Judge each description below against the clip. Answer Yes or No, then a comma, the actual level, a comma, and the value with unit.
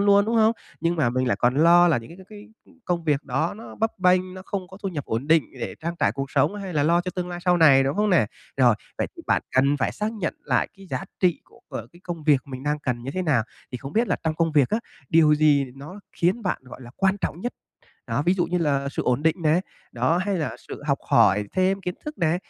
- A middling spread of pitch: Yes, average, 5.0 semitones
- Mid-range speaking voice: Yes, medium, 165 Hz